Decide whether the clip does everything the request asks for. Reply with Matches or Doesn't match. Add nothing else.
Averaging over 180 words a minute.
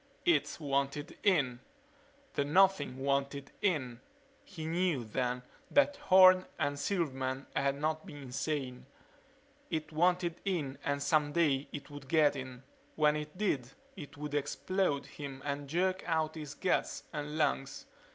Doesn't match